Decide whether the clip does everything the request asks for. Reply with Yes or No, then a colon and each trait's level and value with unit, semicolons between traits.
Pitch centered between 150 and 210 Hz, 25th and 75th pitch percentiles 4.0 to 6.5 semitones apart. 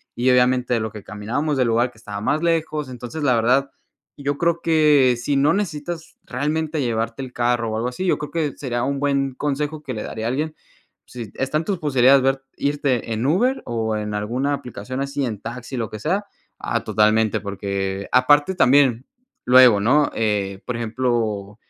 No: low, 125 Hz; average, 4.3 semitones